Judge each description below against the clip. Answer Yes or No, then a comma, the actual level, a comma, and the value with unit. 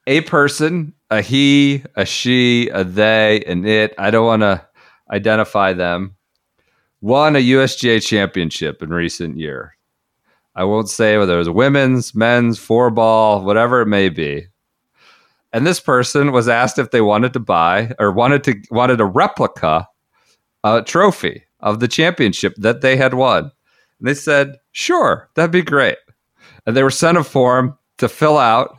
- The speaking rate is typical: Yes, average, 160 wpm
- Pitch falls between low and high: No, low, 120 Hz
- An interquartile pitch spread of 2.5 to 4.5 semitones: No, average, 4.9 semitones